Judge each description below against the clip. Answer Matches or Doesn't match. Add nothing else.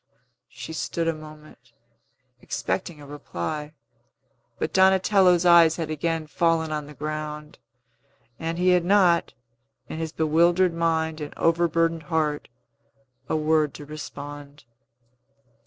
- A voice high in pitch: Doesn't match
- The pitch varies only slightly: Matches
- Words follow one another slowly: Matches